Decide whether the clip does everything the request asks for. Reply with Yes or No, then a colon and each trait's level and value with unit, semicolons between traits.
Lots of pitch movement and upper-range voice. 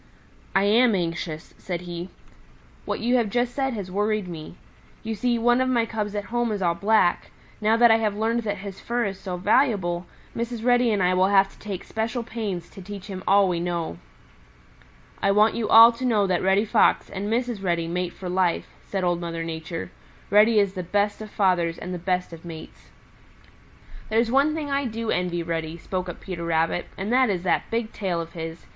No: average, 4.4 semitones; high, 200 Hz